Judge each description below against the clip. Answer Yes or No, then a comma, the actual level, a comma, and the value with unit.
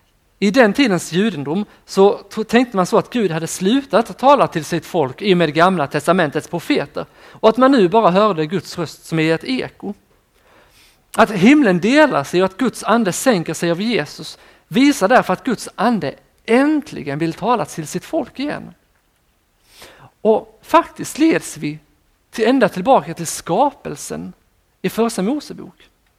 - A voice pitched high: Yes, high, 195 Hz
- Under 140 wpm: No, average, 160 wpm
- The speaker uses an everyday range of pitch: No, wide, 6.7 semitones